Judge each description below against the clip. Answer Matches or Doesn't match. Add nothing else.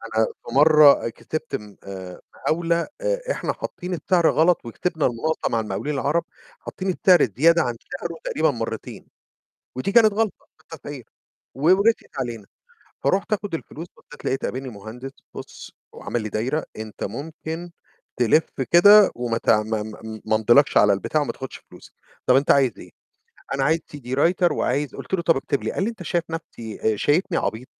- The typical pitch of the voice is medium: Matches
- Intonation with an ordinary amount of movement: Doesn't match